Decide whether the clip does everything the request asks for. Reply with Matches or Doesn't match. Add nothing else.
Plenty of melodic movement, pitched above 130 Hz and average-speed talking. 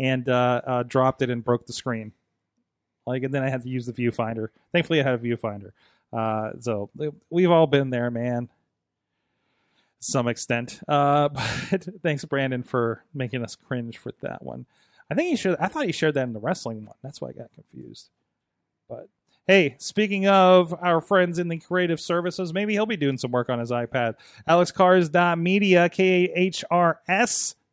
Matches